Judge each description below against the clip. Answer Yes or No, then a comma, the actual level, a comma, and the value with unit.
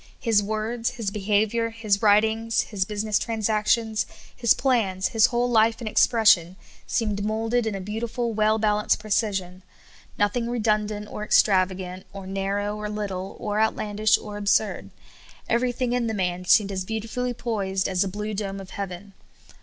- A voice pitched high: Yes, high, 210 Hz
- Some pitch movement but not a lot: No, narrow, 2.2 semitones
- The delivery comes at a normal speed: Yes, average, 155 wpm